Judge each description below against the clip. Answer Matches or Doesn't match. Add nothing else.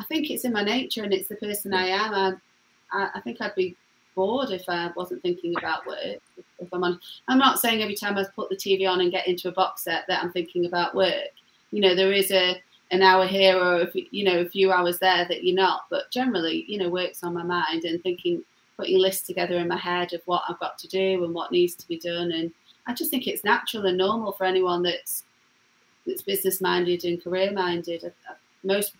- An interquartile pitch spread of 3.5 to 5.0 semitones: Doesn't match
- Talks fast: Matches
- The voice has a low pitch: Doesn't match